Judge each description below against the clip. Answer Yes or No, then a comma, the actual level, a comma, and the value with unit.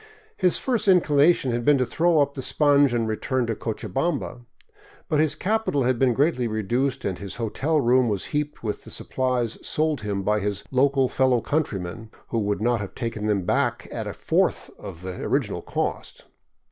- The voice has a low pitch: Yes, low, 125 Hz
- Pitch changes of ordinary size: Yes, average, 5.0 semitones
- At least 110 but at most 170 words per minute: No, average, 185 wpm